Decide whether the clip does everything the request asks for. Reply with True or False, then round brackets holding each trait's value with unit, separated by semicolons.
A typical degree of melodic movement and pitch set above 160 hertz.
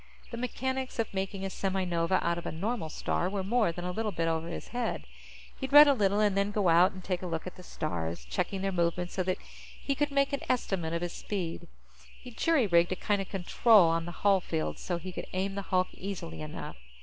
True (3.7 semitones; 190 Hz)